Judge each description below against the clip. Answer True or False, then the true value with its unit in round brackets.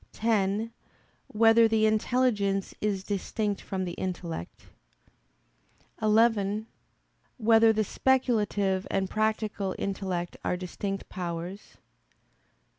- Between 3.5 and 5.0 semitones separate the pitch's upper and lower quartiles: False (2.6 semitones)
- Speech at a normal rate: False (90 wpm)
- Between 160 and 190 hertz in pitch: False (205 Hz)